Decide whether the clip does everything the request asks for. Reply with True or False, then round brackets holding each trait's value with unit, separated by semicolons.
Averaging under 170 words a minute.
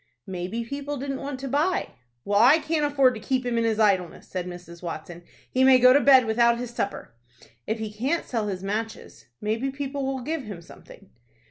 False (205 wpm)